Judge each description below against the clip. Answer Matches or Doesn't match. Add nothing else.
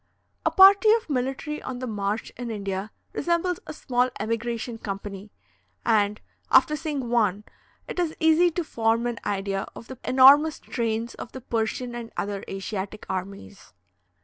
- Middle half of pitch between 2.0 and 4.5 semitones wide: Doesn't match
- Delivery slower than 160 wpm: Matches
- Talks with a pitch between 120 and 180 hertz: Doesn't match